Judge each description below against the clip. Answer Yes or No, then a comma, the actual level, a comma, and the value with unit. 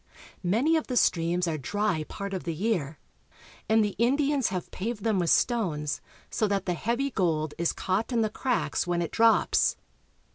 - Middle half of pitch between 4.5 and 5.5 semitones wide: Yes, average, 5.1 semitones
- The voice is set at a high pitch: Yes, high, 200 Hz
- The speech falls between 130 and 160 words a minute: No, average, 185 wpm